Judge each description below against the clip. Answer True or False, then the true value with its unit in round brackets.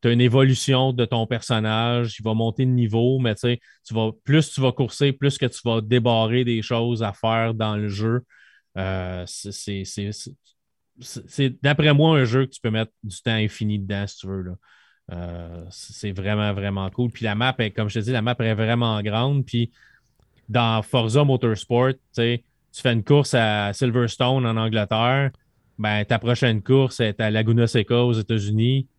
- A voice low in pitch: True (115 Hz)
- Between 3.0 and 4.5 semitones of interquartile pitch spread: False (2.6 semitones)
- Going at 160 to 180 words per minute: False (195 wpm)